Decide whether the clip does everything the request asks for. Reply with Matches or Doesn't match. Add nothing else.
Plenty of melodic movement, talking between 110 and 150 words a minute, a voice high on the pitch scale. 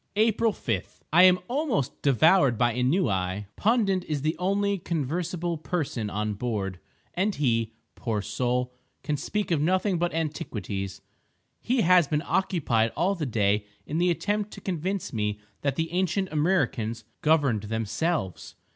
Doesn't match